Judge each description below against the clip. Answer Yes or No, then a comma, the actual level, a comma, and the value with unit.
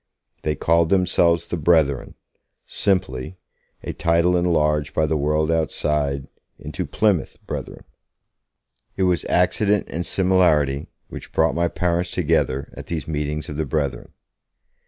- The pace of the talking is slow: Yes, slow, 130 wpm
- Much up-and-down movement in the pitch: No, average, 2.8 semitones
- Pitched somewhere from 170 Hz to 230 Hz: No, very low, 80 Hz